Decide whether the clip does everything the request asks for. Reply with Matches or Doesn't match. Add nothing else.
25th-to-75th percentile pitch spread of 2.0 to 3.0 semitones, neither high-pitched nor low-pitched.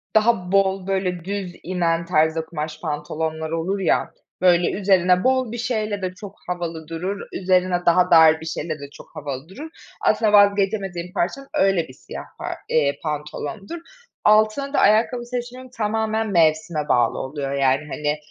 Doesn't match